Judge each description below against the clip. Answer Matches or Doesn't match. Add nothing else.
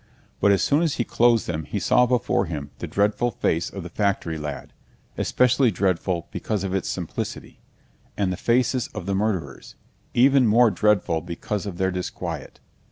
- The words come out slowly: Doesn't match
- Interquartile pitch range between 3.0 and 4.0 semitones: Doesn't match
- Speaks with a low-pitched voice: Matches